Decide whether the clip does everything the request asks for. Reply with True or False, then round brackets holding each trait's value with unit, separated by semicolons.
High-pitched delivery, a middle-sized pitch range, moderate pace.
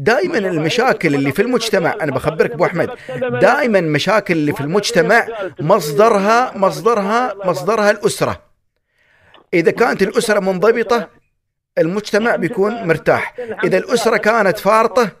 True (210 Hz; 3.9 semitones; 115 wpm)